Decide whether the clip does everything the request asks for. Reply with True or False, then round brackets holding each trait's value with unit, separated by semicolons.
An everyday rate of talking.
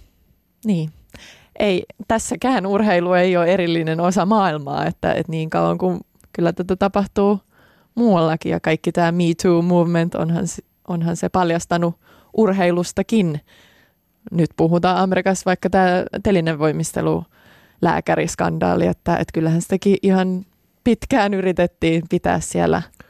True (120 wpm)